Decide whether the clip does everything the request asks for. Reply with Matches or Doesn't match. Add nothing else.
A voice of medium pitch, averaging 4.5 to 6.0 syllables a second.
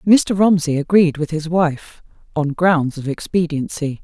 Doesn't match